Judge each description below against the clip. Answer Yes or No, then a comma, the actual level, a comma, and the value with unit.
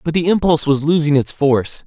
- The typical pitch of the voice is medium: Yes, medium, 150 Hz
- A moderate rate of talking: No, fast, 225 wpm